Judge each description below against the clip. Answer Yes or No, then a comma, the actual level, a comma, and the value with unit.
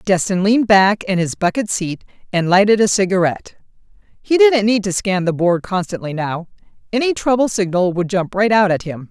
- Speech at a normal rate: Yes, average, 190 wpm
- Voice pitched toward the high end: Yes, high, 195 Hz